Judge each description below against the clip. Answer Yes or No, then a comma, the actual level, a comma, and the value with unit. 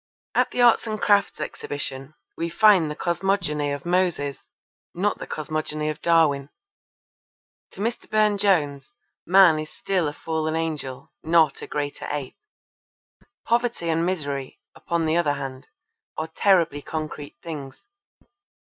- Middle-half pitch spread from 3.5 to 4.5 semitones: Yes, average, 4.2 semitones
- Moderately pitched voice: Yes, medium, 160 Hz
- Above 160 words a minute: No, slow, 135 wpm